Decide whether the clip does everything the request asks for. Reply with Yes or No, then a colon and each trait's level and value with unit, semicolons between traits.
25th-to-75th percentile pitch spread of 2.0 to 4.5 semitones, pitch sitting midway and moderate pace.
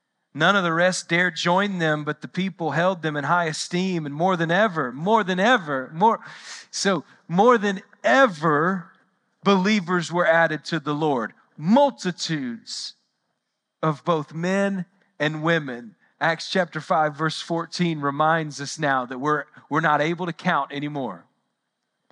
Yes: average, 3.7 semitones; medium, 170 Hz; average, 150 wpm